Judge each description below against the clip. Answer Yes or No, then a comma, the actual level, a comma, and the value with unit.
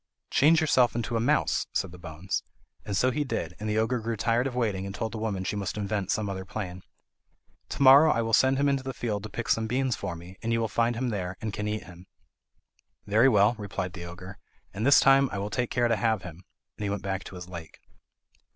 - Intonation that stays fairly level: No, average, 4.1 semitones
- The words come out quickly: Yes, fast, 245 wpm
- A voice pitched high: No, low, 110 Hz